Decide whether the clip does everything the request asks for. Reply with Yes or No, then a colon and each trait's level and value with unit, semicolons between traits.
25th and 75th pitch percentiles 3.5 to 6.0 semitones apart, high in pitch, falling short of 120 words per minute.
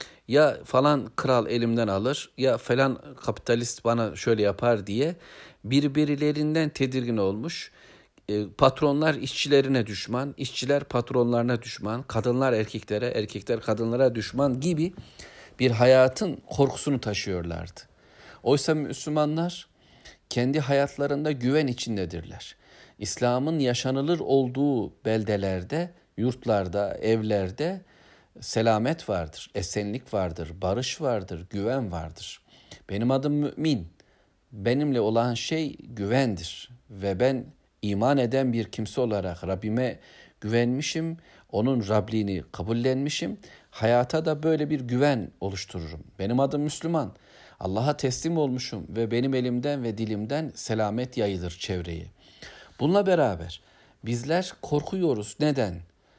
No: average, 5.3 semitones; low, 125 Hz; average, 100 wpm